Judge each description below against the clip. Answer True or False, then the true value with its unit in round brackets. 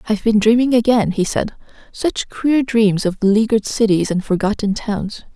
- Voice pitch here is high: True (215 Hz)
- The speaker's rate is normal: True (170 wpm)